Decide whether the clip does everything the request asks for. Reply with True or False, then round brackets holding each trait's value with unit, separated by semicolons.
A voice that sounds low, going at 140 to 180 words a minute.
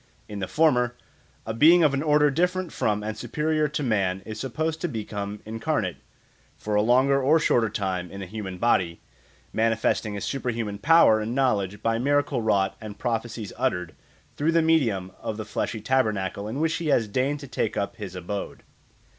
False (115 Hz; 190 wpm)